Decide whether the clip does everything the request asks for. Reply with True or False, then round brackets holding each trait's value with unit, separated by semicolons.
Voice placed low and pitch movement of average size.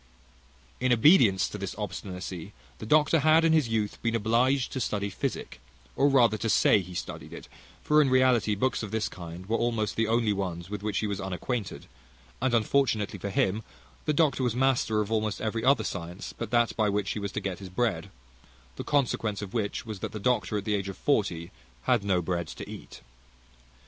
True (110 Hz; 3.8 semitones)